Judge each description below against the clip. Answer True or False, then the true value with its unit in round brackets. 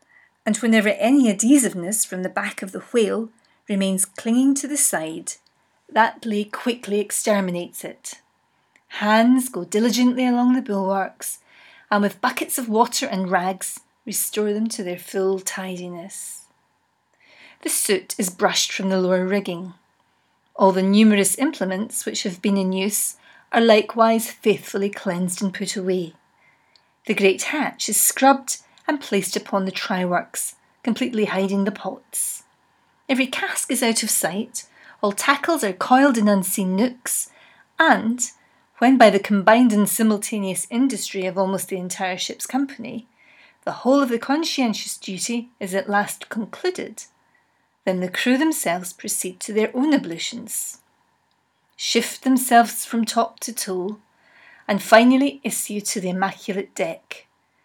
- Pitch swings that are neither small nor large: True (4.5 semitones)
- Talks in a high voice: True (215 Hz)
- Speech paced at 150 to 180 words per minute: False (140 wpm)